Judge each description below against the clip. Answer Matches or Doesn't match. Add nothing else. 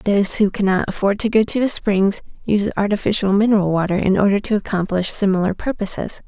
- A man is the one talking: Doesn't match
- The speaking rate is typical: Matches